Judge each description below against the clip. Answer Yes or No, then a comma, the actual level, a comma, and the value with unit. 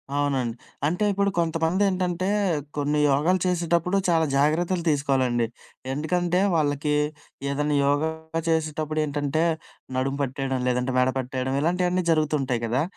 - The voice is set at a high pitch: No, medium, 150 Hz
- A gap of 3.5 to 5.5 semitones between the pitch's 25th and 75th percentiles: Yes, average, 3.9 semitones